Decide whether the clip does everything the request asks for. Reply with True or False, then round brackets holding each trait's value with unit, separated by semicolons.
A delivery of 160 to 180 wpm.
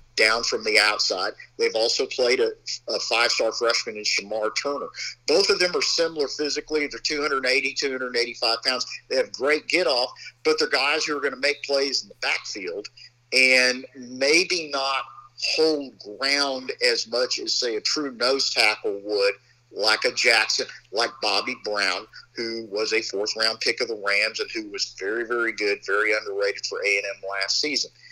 True (175 wpm)